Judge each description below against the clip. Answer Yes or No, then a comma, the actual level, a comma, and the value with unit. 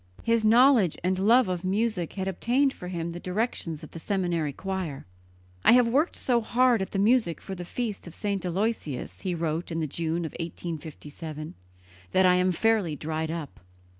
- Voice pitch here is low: No, medium, 185 Hz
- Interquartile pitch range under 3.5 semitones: No, average, 5.1 semitones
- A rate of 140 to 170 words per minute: No, average, 185 wpm